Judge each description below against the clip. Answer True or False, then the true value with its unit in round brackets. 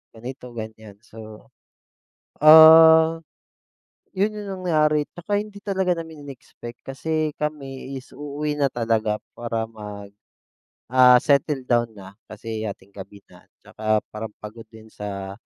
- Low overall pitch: True (125 Hz)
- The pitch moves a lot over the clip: True (6.1 semitones)